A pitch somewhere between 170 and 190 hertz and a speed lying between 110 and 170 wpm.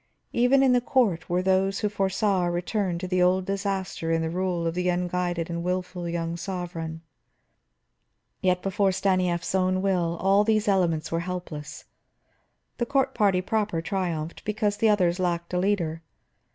Yes: medium, 185 Hz; average, 160 wpm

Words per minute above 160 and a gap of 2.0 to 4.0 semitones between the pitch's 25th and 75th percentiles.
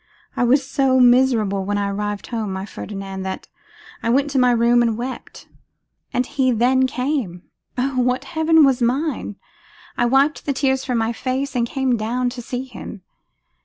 Yes: average, 175 wpm; average, 2.9 semitones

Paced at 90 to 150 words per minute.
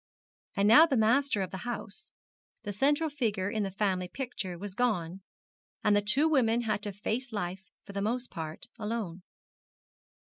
No: average, 170 wpm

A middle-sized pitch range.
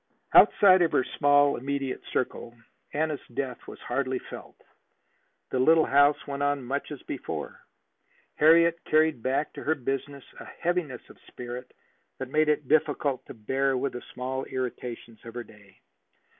Yes: average, 3.0 semitones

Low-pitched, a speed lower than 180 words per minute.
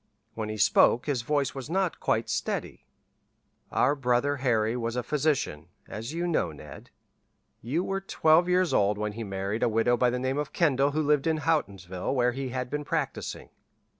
No: low, 130 Hz; average, 185 wpm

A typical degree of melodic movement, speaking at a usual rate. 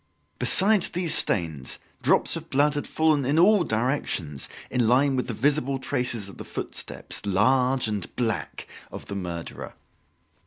No: wide, 6.1 semitones; average, 150 wpm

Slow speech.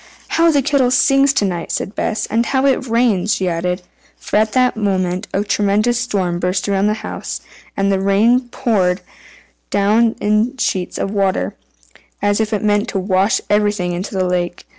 No: average, 180 wpm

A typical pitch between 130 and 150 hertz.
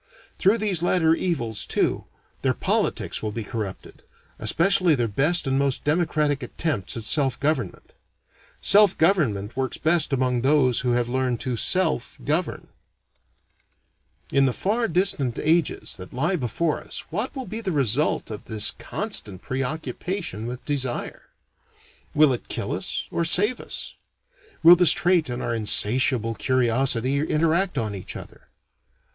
Yes: medium, 140 Hz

